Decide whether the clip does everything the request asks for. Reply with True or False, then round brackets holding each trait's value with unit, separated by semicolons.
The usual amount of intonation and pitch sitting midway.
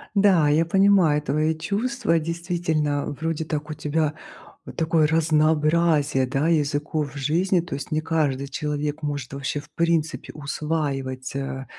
False (2.1 semitones; 155 Hz)